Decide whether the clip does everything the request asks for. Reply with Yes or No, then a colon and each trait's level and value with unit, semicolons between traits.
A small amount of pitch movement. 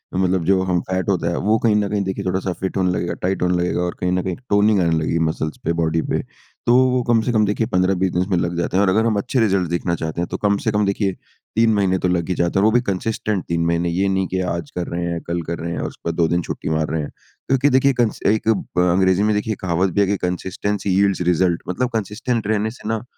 No: average, 3.2 semitones